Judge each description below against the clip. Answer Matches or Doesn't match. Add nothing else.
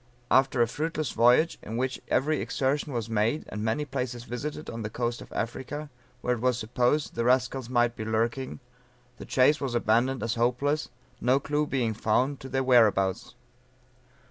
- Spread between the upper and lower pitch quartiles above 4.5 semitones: Doesn't match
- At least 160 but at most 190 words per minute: Matches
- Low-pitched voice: Matches